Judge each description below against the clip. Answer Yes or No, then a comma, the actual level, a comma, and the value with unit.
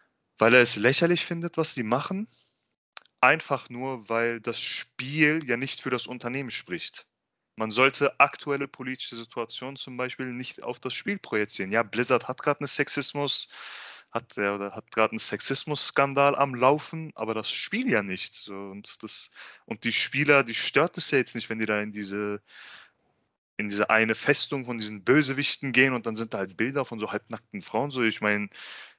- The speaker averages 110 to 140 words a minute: No, average, 180 wpm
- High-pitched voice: No, low, 125 Hz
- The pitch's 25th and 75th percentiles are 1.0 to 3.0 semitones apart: No, average, 4.0 semitones